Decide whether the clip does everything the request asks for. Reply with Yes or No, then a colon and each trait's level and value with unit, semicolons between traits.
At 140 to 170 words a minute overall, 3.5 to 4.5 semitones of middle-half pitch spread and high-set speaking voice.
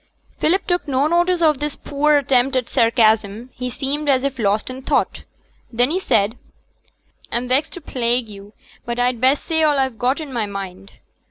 No: average, 185 wpm; average, 4.1 semitones; very high, 255 Hz